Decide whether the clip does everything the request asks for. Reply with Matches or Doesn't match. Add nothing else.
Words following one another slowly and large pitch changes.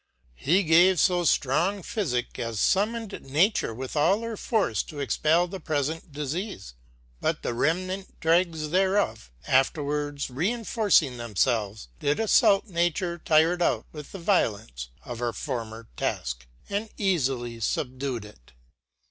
Matches